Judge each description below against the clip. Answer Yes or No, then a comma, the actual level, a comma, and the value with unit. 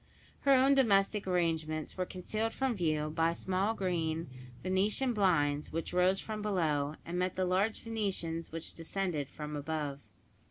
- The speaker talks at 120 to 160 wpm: Yes, average, 150 wpm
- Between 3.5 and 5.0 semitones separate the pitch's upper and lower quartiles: Yes, average, 4.1 semitones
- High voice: No, medium, 180 Hz